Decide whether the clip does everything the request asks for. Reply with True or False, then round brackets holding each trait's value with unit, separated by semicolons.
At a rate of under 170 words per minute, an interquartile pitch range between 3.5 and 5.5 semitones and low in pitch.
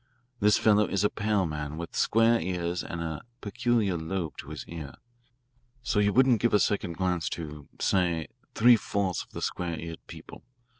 False (180 wpm; 4.0 semitones; 95 Hz)